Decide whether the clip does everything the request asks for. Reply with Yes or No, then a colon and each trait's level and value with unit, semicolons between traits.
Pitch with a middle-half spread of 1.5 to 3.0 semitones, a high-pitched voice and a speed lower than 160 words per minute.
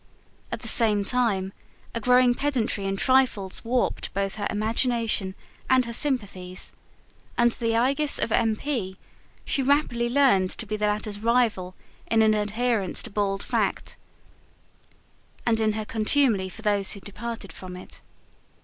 No: average, 3.4 semitones; high, 220 Hz; average, 150 wpm